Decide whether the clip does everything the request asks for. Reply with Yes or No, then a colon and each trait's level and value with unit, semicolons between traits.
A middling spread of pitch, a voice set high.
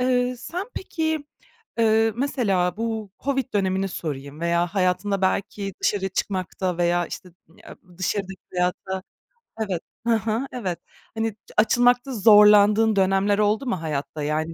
Yes: average, 3.8 semitones; high, 200 Hz